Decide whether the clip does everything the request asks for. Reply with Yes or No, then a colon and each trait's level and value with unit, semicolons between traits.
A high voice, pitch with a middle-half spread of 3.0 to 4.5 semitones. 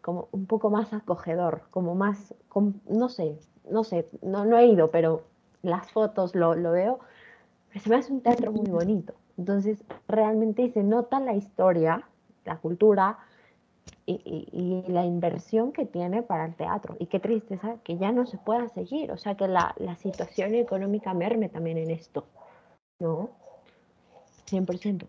Yes: high, 200 Hz; average, 4.2 semitones